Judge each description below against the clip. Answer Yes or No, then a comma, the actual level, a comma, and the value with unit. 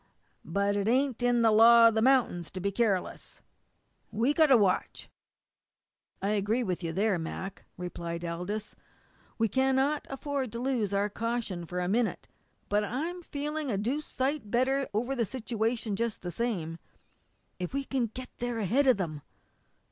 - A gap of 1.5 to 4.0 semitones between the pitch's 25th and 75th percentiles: No, average, 4.7 semitones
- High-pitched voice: Yes, high, 225 Hz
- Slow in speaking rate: No, average, 170 wpm